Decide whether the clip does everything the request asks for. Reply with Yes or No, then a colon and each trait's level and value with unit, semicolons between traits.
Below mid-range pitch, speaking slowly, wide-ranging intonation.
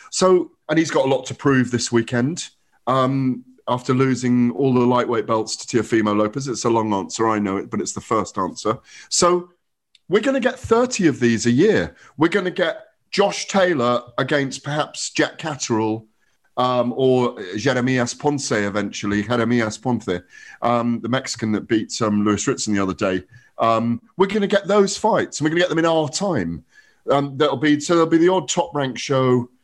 No: low, 130 Hz; average, 195 wpm; wide, 5.8 semitones